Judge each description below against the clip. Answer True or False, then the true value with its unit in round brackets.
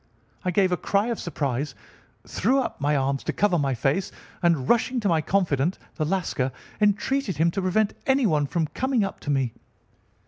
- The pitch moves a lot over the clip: True (6.2 semitones)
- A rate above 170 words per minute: True (180 wpm)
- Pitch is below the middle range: False (175 Hz)